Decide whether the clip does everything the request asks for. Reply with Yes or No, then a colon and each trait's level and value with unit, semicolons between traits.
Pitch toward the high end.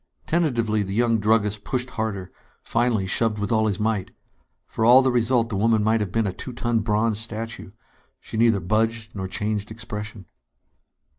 No: low, 110 Hz